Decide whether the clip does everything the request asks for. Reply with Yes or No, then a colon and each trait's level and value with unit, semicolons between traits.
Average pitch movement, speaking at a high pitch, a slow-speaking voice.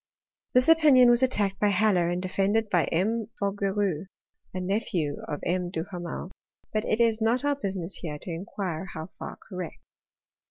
No: average, 3.9 semitones; high, 195 Hz; average, 155 wpm